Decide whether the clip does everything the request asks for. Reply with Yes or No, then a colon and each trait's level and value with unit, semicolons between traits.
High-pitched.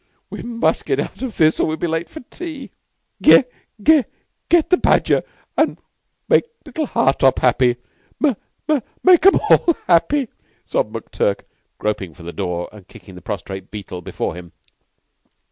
No: low, 135 Hz